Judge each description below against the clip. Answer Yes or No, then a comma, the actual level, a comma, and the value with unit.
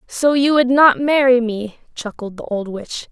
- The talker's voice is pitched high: Yes, very high, 250 Hz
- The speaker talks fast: No, average, 190 wpm